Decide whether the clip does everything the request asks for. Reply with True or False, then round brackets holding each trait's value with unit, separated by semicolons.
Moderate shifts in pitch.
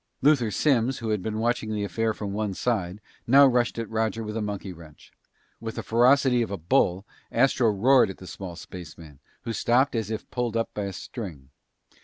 True (3.5 semitones)